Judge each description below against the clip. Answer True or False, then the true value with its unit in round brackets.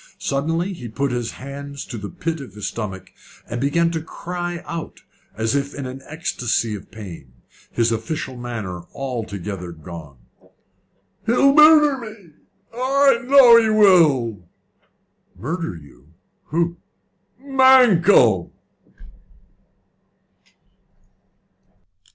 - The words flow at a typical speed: False (105 wpm)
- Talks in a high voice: False (140 Hz)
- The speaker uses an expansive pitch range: True (8.5 semitones)